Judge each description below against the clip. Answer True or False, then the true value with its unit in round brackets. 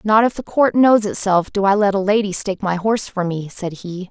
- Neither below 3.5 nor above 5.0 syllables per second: False (5.5 syllables/s)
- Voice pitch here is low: False (200 Hz)